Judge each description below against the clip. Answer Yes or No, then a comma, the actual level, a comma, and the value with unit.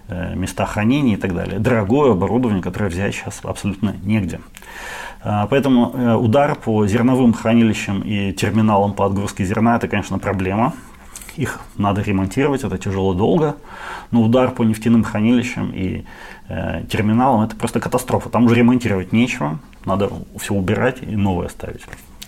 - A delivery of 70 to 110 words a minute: No, average, 135 wpm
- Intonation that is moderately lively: Yes, average, 3.3 semitones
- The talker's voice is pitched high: No, low, 110 Hz